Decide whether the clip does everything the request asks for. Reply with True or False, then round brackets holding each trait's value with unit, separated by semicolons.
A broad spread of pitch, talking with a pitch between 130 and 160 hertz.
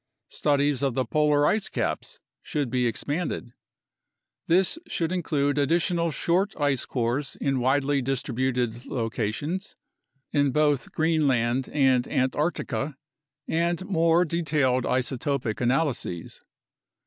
False (4.0 semitones; 140 Hz)